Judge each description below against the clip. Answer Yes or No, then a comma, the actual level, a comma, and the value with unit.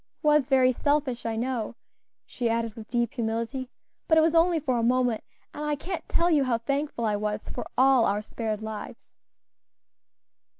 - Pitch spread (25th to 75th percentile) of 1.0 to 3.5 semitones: No, average, 4.2 semitones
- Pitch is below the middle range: No, very high, 250 Hz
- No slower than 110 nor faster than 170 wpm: No, average, 180 wpm